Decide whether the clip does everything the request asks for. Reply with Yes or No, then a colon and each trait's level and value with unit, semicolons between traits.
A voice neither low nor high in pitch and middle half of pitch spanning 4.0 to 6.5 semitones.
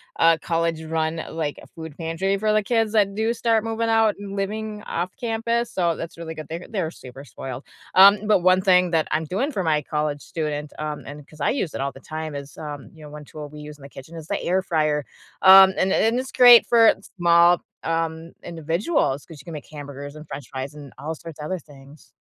Yes: medium, 165 Hz; average, 4.7 semitones